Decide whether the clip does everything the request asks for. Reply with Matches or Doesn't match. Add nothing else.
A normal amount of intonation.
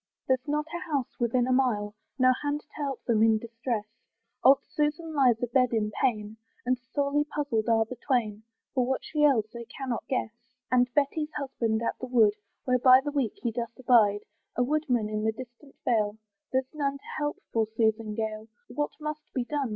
Matches